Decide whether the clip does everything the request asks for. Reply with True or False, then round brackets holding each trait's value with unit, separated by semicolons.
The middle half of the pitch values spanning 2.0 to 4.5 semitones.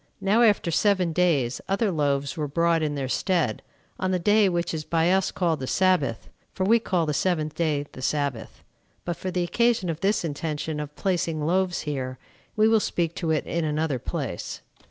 True (3.9 semitones)